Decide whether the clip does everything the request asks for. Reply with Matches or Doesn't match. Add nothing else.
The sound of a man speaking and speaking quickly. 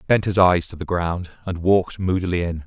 Matches